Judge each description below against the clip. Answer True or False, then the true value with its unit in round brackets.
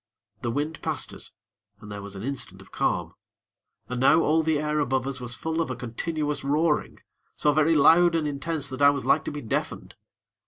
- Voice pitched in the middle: True (145 Hz)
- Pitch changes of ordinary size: True (3.3 semitones)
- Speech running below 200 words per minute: False (205 wpm)